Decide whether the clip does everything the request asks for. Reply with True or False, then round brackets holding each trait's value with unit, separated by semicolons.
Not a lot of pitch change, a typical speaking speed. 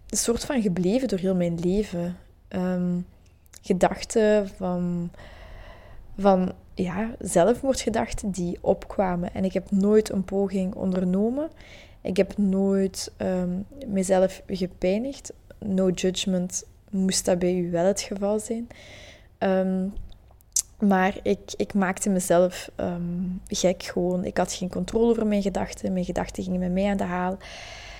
False (2.1 semitones; 130 wpm)